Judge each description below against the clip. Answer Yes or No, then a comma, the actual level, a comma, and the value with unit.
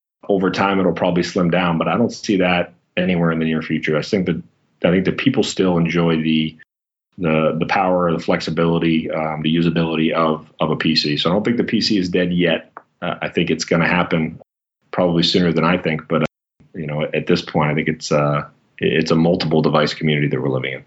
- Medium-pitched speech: No, very low, 80 Hz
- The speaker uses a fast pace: Yes, fast, 225 wpm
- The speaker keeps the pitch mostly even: Yes, narrow, 1.8 semitones